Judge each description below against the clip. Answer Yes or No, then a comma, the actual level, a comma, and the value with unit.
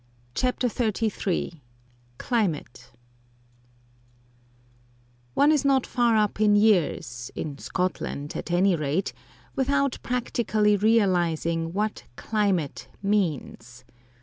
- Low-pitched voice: No, high, 200 Hz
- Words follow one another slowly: Yes, slow, 90 wpm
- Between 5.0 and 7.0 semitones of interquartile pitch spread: Yes, wide, 5.5 semitones